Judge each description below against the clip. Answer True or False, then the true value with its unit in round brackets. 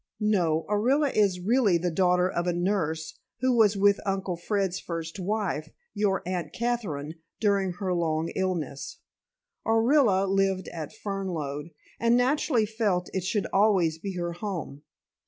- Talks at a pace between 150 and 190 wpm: False (140 wpm)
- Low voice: False (190 Hz)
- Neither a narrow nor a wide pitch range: True (3.5 semitones)